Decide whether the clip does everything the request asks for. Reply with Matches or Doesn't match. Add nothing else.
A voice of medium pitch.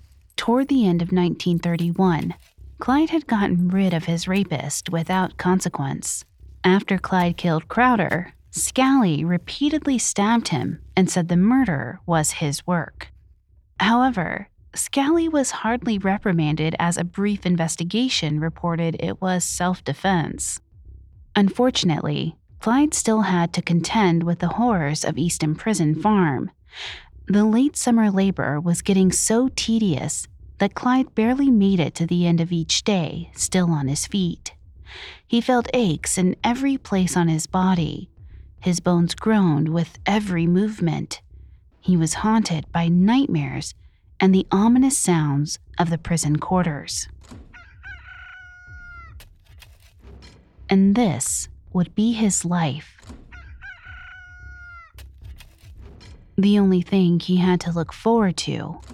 Matches